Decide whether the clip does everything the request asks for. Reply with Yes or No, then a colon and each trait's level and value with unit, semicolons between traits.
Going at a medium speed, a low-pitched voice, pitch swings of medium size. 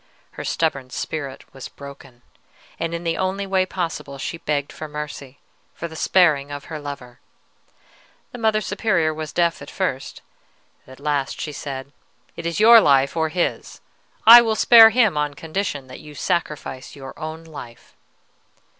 No: average, 160 wpm; medium, 155 Hz; average, 4.4 semitones